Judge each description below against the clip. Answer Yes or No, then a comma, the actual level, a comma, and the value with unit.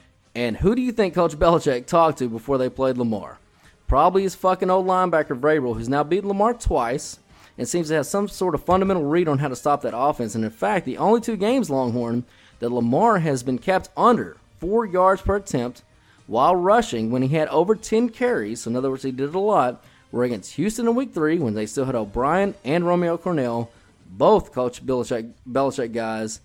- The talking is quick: Yes, fast, 210 wpm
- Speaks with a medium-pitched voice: Yes, medium, 145 Hz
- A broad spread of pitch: Yes, wide, 7.6 semitones